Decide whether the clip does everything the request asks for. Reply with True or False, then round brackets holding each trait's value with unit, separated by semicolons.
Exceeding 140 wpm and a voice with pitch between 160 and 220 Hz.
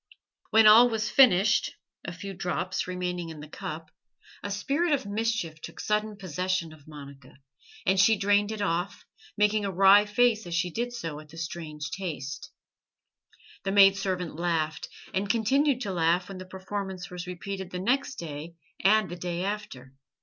True (170 wpm; 190 Hz)